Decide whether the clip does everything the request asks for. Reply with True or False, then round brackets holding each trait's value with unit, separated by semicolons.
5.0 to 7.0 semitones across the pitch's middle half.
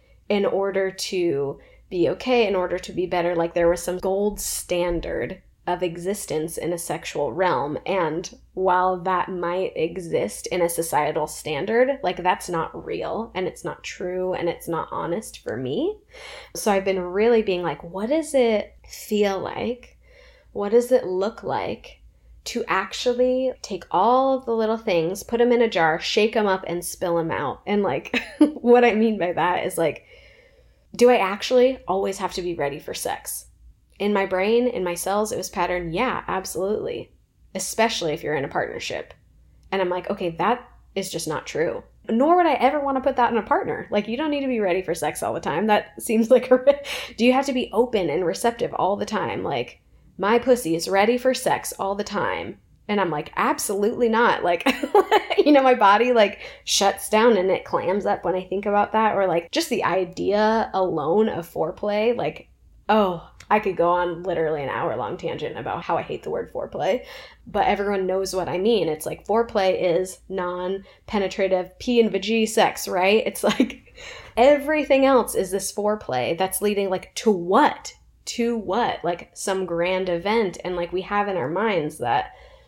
True (5.3 semitones)